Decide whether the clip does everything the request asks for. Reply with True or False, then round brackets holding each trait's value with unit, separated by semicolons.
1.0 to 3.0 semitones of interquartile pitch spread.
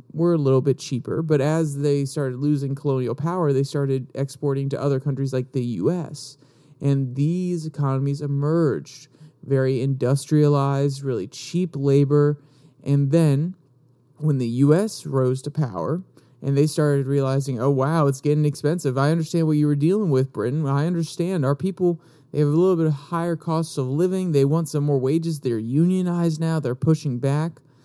True (2.7 semitones)